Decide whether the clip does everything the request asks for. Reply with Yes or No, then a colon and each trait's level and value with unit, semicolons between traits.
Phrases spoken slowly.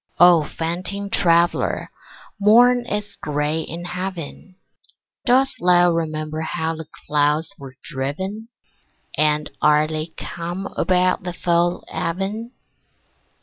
Yes: slow, 110 wpm